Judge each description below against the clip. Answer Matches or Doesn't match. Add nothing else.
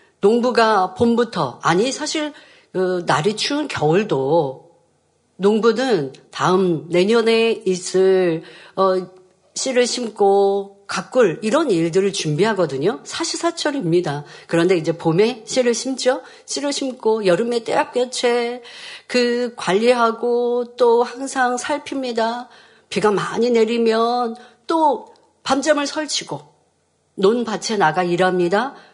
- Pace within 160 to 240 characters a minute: Matches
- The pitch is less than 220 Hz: Doesn't match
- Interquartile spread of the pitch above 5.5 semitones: Doesn't match